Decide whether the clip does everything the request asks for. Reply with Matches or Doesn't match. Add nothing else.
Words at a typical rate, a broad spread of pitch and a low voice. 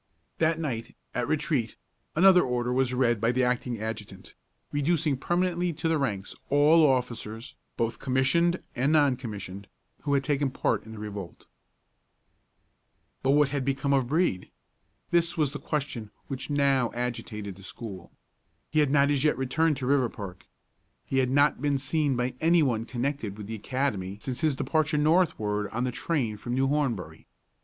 Doesn't match